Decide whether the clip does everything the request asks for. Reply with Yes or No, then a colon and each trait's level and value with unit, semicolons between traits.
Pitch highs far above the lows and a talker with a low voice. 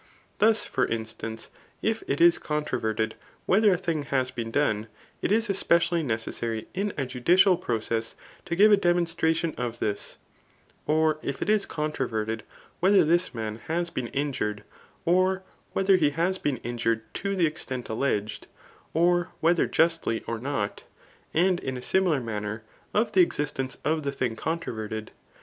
No: wide, 7.2 semitones; medium, 150 Hz